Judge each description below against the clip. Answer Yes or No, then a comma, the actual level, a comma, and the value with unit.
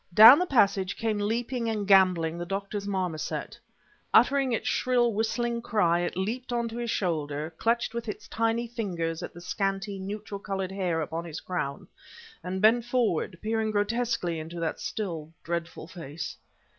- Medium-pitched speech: No, high, 200 Hz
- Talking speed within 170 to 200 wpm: No, average, 155 wpm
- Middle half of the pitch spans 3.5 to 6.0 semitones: Yes, average, 4.9 semitones